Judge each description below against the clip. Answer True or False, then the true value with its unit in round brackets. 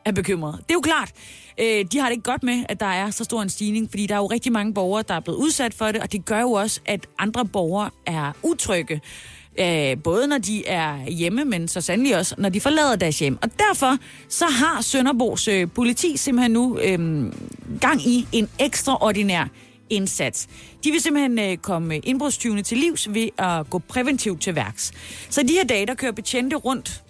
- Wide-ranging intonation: True (5.7 semitones)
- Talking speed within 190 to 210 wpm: True (200 wpm)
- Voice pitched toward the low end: False (215 Hz)